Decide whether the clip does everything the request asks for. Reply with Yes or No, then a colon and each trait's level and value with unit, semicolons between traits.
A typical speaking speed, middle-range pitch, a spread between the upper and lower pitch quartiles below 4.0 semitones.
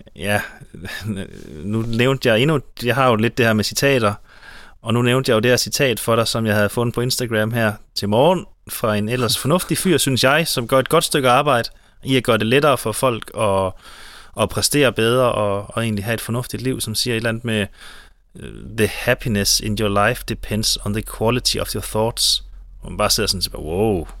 No: average, 215 wpm; low, 115 Hz; average, 3.1 semitones